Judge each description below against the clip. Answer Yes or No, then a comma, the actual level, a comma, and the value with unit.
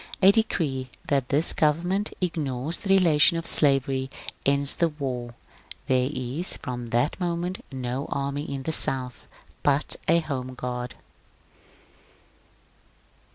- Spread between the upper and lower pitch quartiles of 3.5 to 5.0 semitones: Yes, average, 4.5 semitones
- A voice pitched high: No, medium, 140 Hz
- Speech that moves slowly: Yes, slow, 125 wpm